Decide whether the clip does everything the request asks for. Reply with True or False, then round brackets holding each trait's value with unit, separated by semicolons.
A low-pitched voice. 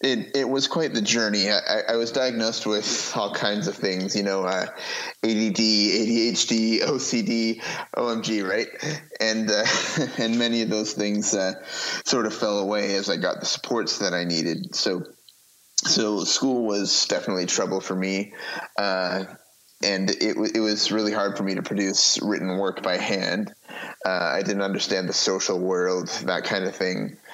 True (105 Hz)